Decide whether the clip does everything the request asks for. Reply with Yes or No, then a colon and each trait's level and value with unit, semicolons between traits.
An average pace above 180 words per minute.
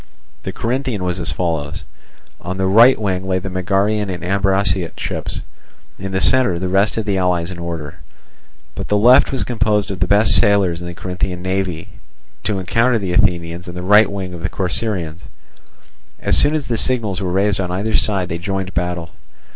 Yes: average, 190 wpm